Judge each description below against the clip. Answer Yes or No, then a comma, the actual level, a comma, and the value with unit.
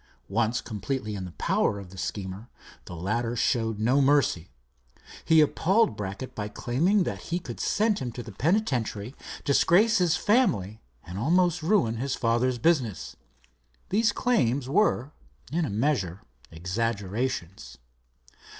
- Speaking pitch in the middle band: No, low, 120 Hz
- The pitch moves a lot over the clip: Yes, wide, 7.8 semitones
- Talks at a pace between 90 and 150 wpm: Yes, slow, 135 wpm